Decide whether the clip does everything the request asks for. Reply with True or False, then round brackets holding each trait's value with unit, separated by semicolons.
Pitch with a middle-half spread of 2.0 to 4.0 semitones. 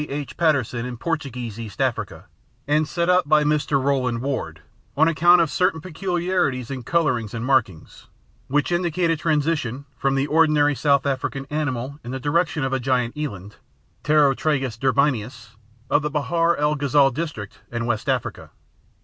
True (3.6 semitones)